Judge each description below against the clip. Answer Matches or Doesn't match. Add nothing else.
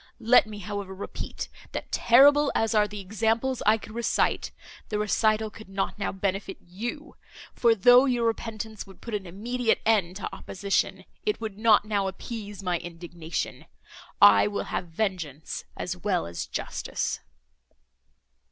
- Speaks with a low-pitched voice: Doesn't match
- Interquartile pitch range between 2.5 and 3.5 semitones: Matches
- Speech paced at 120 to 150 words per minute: Matches